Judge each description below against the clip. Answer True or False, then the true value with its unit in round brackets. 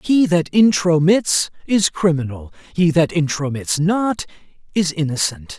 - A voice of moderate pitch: True (165 Hz)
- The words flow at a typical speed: False (120 wpm)